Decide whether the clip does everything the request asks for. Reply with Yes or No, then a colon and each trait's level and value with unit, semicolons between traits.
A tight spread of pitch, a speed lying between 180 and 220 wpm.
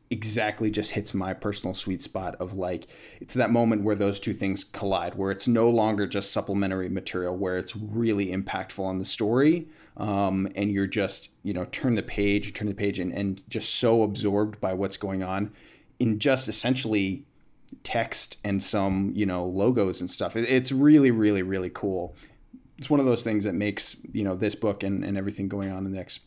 Yes: narrow, 2.2 semitones; average, 200 wpm